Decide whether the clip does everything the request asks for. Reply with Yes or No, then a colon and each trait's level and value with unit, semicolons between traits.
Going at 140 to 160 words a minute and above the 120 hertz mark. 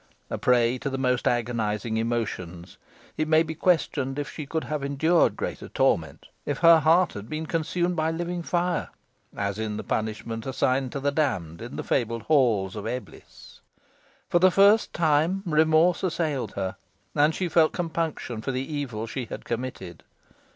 No: average, 170 wpm; medium, 140 Hz